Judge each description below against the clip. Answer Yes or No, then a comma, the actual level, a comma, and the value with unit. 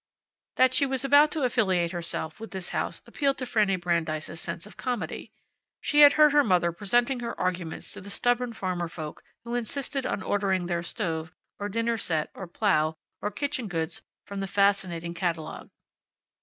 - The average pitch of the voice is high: Yes, high, 200 Hz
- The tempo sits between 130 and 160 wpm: No, average, 175 wpm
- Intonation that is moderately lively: No, wide, 6.0 semitones